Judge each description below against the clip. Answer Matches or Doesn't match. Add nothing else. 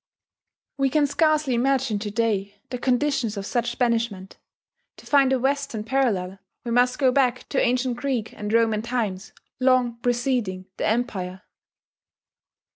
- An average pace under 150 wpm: Matches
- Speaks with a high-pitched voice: Matches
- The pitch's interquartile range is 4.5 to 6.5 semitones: Doesn't match